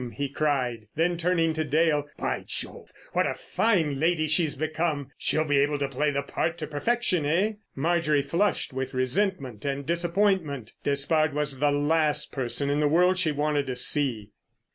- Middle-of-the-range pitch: Yes, medium, 150 Hz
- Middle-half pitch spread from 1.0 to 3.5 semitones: Yes, average, 3.1 semitones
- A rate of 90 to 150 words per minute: No, average, 170 wpm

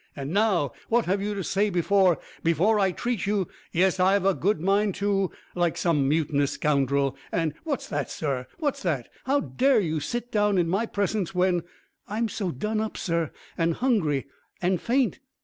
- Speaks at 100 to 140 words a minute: No, average, 185 wpm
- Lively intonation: No, average, 4.4 semitones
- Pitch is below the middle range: No, high, 190 Hz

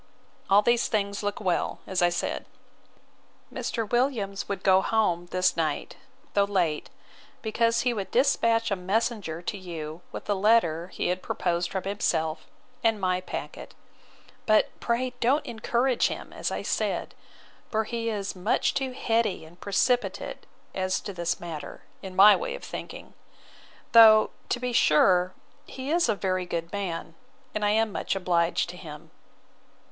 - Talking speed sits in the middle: Yes, average, 155 wpm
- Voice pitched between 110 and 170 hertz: No, high, 200 Hz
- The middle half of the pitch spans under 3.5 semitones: No, average, 4.2 semitones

